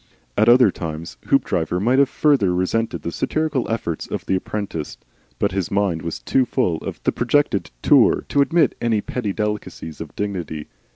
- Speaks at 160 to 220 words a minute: Yes, average, 170 wpm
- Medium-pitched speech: No, low, 105 Hz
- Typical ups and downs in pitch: No, wide, 6.4 semitones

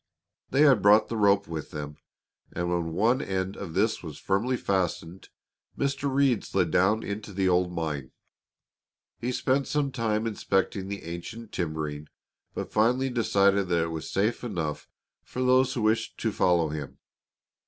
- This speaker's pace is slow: No, average, 160 wpm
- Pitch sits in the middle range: No, low, 100 Hz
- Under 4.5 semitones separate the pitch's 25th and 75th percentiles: No, average, 5.2 semitones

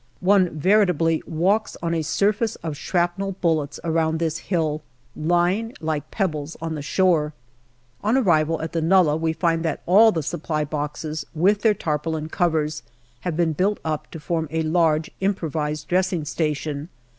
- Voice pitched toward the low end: No, medium, 165 Hz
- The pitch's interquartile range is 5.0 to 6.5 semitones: No, average, 2.8 semitones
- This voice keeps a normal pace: Yes, average, 160 wpm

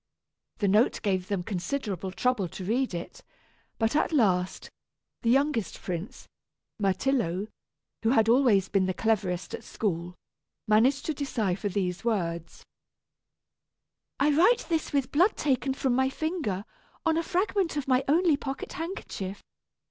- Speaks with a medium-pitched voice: No, high, 230 Hz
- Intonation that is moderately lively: No, wide, 6.8 semitones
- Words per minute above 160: No, average, 140 wpm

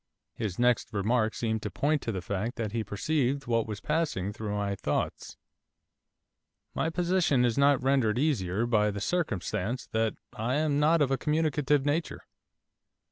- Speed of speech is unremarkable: Yes, average, 160 wpm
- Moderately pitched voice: No, low, 120 Hz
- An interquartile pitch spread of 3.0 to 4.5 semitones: No, wide, 5.5 semitones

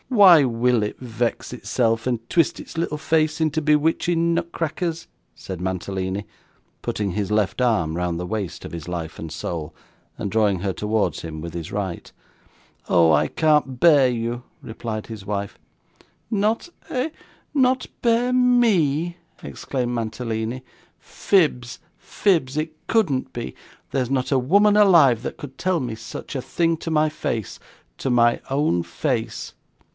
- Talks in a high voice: No, low, 125 Hz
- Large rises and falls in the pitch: Yes, wide, 7.7 semitones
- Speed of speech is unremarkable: Yes, average, 150 wpm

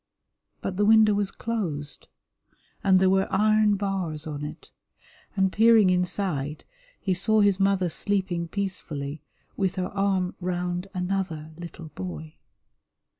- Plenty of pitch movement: No, average, 3.3 semitones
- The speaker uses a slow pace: Yes, slow, 125 wpm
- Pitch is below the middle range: No, medium, 185 Hz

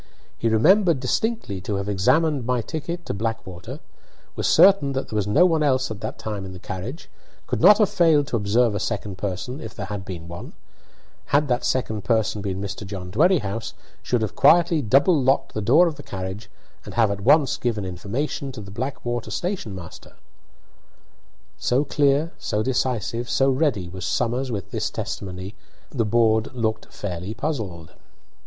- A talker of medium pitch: No, low, 115 Hz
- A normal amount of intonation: No, wide, 5.8 semitones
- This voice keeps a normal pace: Yes, average, 175 wpm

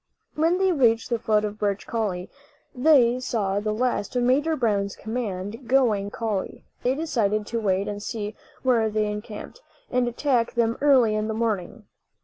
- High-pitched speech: Yes, high, 225 Hz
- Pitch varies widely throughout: No, average, 3.3 semitones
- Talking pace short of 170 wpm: No, average, 175 wpm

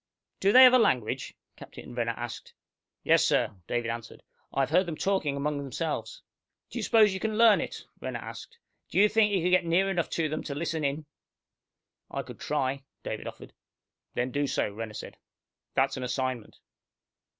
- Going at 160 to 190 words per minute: Yes, average, 185 wpm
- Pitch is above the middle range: No, medium, 150 Hz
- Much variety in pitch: Yes, wide, 6.9 semitones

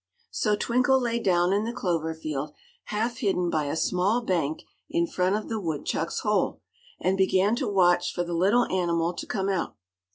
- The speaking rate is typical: Yes, average, 185 wpm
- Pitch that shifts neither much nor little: Yes, average, 4.1 semitones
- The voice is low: No, high, 190 Hz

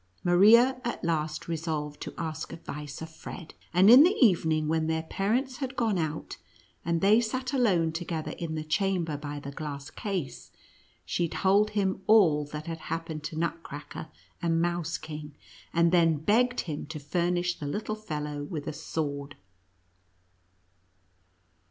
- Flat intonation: No, average, 4.1 semitones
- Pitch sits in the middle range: Yes, medium, 165 Hz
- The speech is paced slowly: No, average, 150 wpm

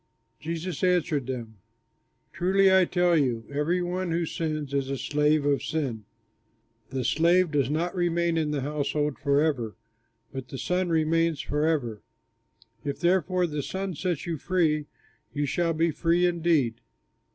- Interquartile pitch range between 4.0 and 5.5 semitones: No, average, 3.5 semitones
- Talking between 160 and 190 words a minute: No, average, 145 wpm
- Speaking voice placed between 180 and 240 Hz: No, medium, 155 Hz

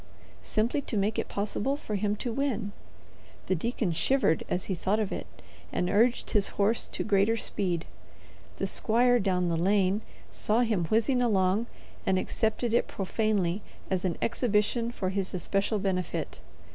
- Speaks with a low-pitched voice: No, high, 205 Hz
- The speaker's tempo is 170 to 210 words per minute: No, average, 160 wpm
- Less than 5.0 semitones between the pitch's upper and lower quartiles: Yes, average, 3.4 semitones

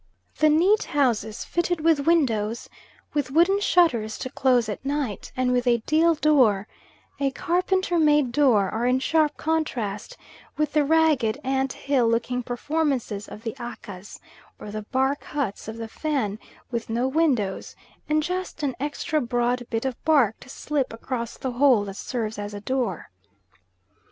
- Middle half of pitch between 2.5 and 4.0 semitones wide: No, average, 5.0 semitones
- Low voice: No, very high, 260 Hz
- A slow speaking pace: No, average, 160 wpm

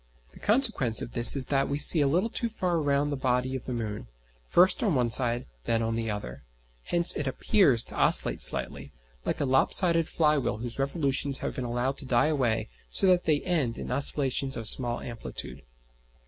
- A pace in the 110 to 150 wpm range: No, fast, 205 wpm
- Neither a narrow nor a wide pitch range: Yes, average, 4.8 semitones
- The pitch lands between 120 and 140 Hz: Yes, low, 135 Hz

